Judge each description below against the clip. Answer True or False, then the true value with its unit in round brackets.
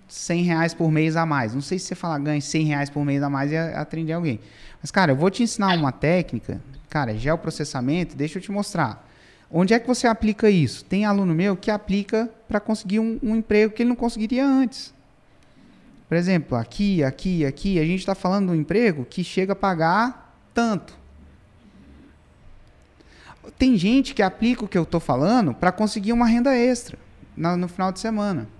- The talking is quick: True (190 wpm)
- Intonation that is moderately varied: False (6.5 semitones)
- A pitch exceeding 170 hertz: True (180 Hz)